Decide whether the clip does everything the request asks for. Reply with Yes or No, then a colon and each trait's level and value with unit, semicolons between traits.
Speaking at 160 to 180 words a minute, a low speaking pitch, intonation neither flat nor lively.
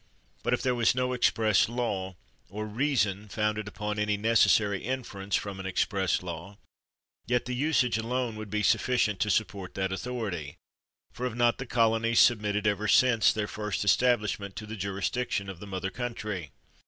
Yes: average, 170 wpm; low, 105 Hz; average, 3.2 semitones